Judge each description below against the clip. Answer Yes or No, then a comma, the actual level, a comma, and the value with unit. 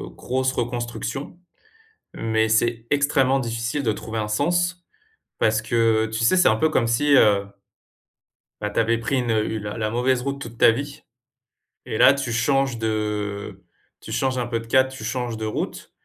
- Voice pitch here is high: No, low, 115 Hz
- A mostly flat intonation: No, average, 3.2 semitones